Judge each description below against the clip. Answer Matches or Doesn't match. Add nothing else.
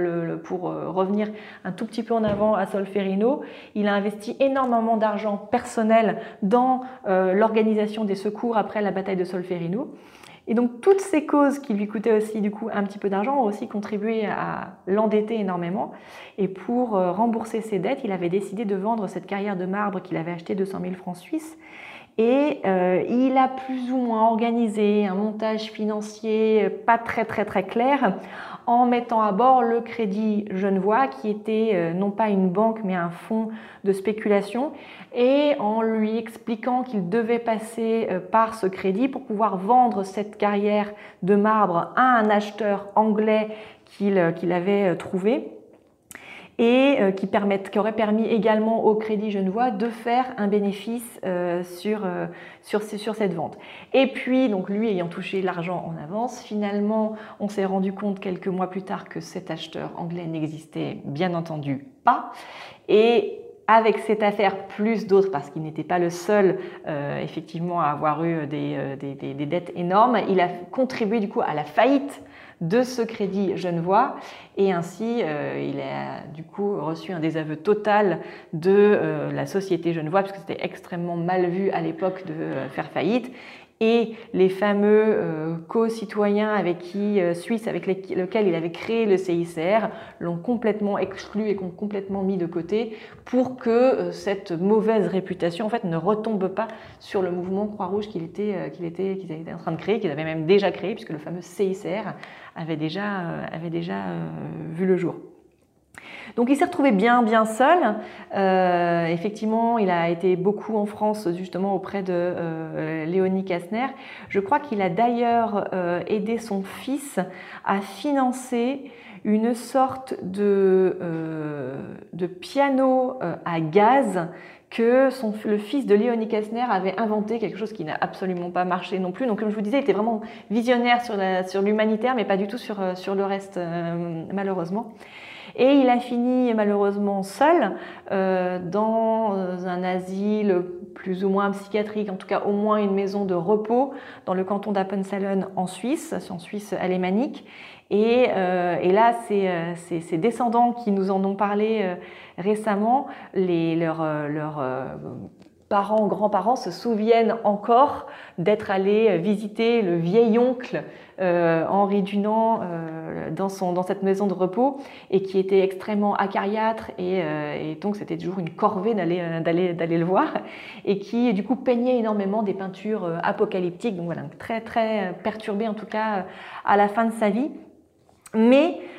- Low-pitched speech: Doesn't match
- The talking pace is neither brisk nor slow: Matches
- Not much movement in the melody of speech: Doesn't match